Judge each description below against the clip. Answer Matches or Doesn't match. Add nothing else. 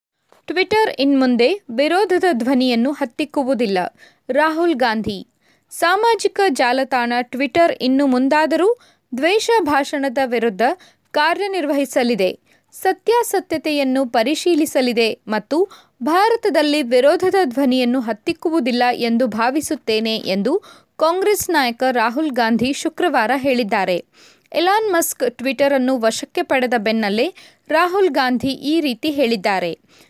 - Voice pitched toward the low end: Doesn't match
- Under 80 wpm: Doesn't match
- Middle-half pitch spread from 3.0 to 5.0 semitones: Doesn't match